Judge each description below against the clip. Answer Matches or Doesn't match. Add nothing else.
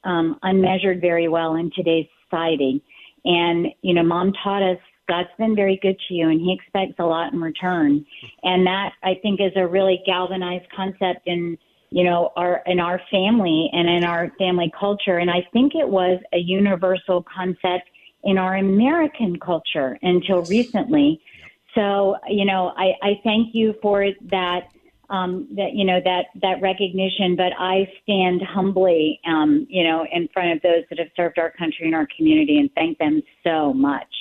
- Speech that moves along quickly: Doesn't match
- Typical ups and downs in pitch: Doesn't match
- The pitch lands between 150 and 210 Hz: Matches